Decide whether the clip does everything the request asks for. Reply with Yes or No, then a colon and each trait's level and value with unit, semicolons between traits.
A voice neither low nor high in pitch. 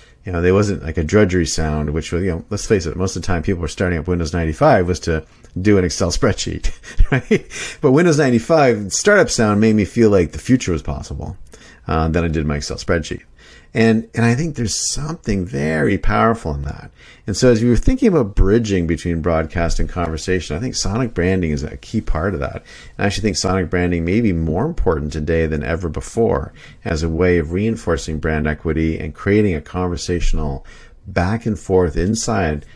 No: very low, 90 Hz